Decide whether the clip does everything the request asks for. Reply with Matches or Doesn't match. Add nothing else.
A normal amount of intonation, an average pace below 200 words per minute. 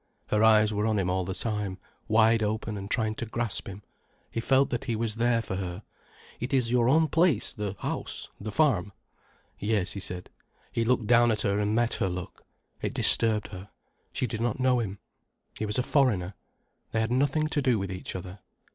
Doesn't match